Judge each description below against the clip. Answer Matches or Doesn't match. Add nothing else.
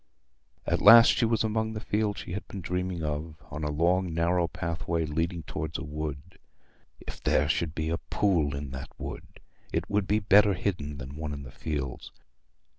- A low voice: Matches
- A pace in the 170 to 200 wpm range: Matches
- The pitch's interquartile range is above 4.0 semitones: Matches